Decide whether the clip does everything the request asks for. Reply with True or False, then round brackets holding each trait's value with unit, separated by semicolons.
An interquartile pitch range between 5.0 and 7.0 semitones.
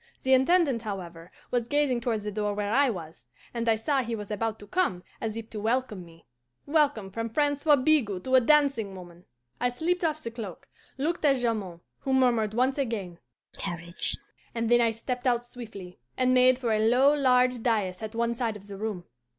False (4.0 semitones)